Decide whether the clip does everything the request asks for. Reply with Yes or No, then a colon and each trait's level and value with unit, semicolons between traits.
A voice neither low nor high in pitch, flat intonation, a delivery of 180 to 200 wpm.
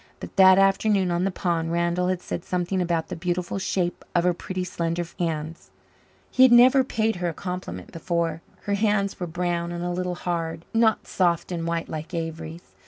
Yes: medium, 175 Hz; narrow, 2.0 semitones; average, 190 wpm